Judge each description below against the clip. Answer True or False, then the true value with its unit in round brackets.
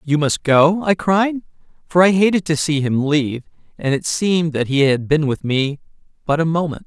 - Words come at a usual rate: False (210 wpm)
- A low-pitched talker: False (155 Hz)